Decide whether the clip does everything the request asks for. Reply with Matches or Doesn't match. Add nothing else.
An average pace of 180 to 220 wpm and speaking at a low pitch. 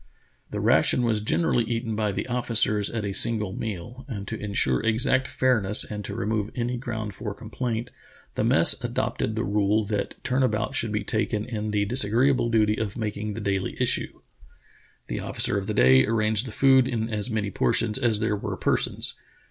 Matches